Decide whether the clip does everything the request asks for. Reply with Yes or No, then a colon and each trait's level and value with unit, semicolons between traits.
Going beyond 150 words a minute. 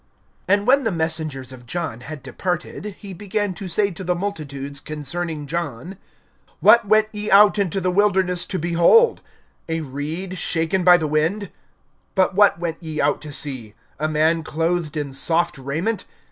Yes: average, 165 wpm